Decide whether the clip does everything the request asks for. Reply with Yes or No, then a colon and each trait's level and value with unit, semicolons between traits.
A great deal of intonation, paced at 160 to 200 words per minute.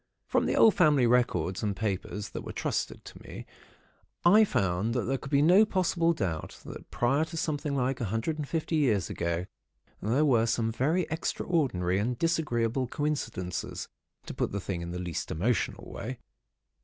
Yes: wide, 7.4 semitones; average, 175 wpm